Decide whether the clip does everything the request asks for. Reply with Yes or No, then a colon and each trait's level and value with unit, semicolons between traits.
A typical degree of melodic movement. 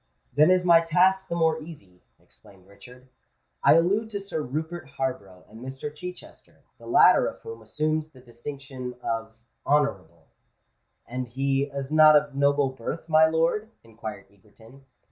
Yes: average, 4.7 semitones